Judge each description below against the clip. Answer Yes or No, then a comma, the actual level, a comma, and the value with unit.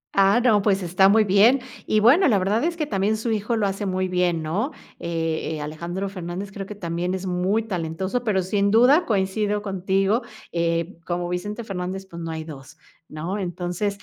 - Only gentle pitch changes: No, average, 3.1 semitones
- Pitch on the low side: No, high, 195 Hz